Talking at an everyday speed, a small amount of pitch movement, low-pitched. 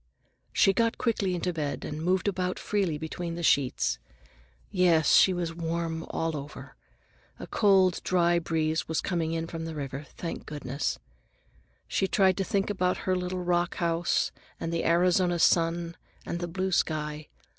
No: average, 160 wpm; narrow, 2.2 semitones; medium, 170 Hz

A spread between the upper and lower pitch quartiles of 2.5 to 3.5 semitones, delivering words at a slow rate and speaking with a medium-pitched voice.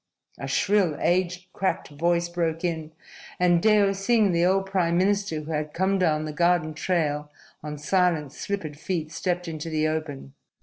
No: average, 3.2 semitones; average, 165 wpm; medium, 170 Hz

